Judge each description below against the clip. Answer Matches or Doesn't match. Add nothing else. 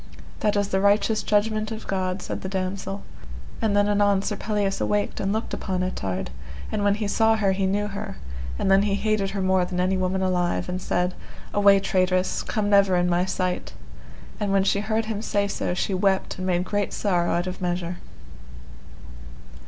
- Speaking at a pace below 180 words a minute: Doesn't match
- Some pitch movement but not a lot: Doesn't match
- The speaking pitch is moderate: Doesn't match